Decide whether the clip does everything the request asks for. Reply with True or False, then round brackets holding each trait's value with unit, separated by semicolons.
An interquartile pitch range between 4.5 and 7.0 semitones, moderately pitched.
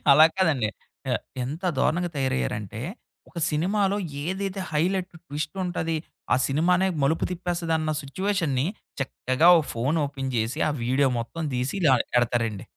True (5.2 semitones; 155 Hz)